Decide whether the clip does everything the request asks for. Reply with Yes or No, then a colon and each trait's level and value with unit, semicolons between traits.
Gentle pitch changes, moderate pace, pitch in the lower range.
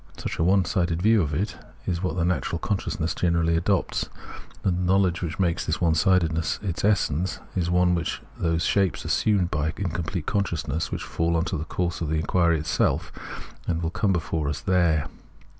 Yes: narrow, 2.2 semitones; average, 190 wpm; very low, 85 Hz